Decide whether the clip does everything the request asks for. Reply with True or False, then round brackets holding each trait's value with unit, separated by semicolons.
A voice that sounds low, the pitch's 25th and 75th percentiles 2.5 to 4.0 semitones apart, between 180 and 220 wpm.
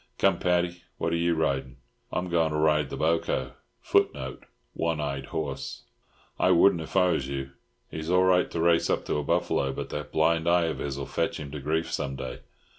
True (80 Hz; 3.5 semitones; 195 wpm)